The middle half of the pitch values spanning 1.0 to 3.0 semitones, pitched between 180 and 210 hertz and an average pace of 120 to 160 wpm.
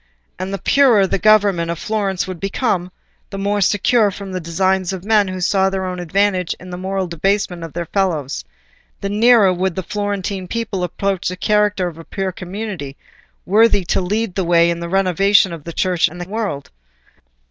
No: narrow, 2.4 semitones; high, 190 Hz; average, 185 wpm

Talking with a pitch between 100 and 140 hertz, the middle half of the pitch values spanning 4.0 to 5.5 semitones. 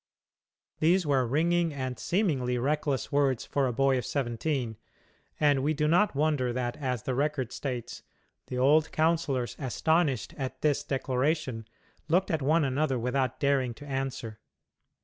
No: low, 135 Hz; average, 3.2 semitones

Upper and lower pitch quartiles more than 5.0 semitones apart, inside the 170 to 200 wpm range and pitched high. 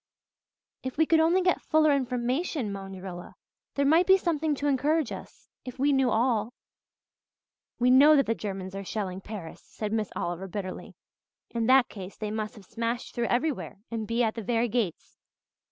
Yes: wide, 5.4 semitones; average, 180 wpm; high, 235 Hz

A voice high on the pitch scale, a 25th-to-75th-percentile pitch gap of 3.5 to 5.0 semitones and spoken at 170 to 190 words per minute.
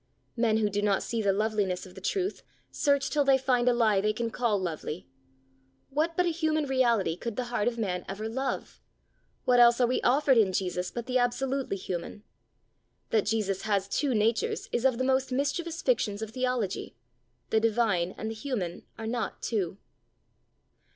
Yes: high, 230 Hz; average, 4.2 semitones; average, 185 wpm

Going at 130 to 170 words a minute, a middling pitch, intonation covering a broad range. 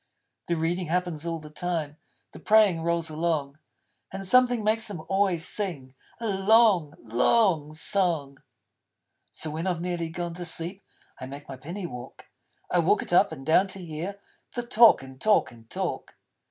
No: average, 165 wpm; medium, 170 Hz; average, 4.2 semitones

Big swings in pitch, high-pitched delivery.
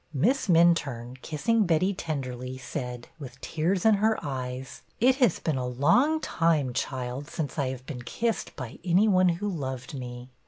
No: wide, 6.4 semitones; medium, 145 Hz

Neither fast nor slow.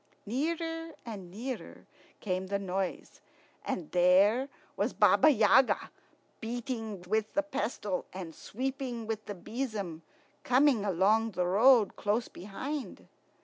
No: slow, 115 wpm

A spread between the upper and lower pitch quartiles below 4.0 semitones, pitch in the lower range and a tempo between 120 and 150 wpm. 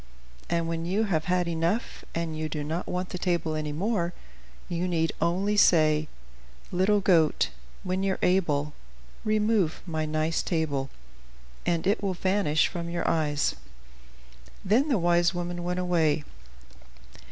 No: average, 2.9 semitones; medium, 170 Hz; average, 140 wpm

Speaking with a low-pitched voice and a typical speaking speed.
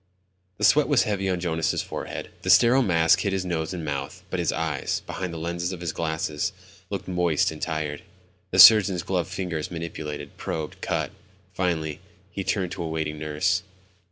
Yes: very low, 85 Hz; average, 180 wpm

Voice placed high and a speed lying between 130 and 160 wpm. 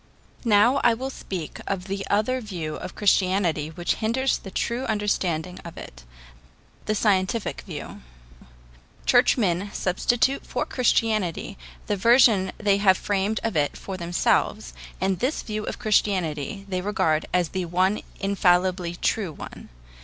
Yes: high, 195 Hz; average, 140 wpm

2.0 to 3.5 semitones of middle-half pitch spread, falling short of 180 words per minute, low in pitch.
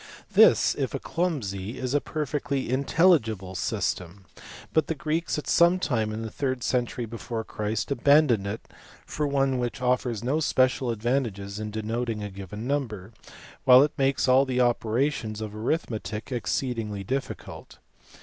No: average, 4.4 semitones; average, 150 wpm; low, 125 Hz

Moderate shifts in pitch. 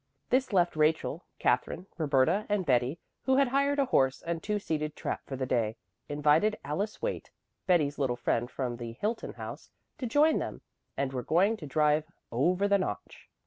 No: wide, 7.6 semitones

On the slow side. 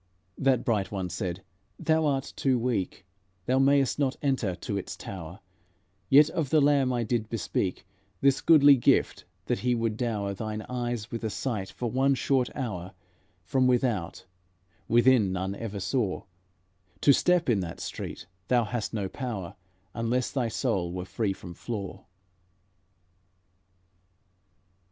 No: average, 145 wpm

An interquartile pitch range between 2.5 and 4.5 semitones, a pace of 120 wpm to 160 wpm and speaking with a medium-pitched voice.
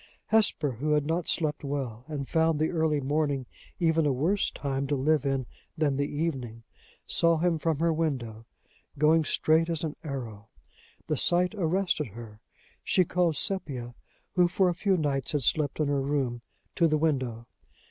No: average, 3.3 semitones; average, 170 wpm; medium, 150 Hz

